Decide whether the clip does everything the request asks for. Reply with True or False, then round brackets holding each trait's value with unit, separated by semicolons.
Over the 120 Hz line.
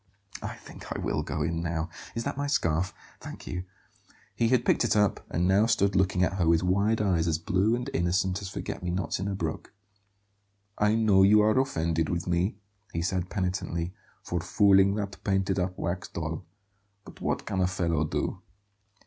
False (95 Hz)